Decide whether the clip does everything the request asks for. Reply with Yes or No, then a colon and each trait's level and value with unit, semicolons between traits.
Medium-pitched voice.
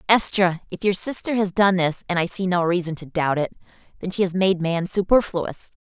Yes: medium, 180 Hz